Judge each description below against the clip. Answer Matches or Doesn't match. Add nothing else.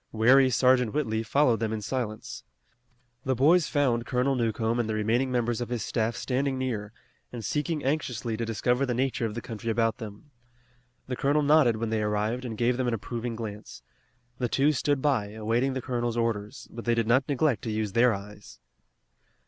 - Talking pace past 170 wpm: Matches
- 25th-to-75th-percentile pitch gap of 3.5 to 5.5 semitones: Doesn't match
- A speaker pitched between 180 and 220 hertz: Doesn't match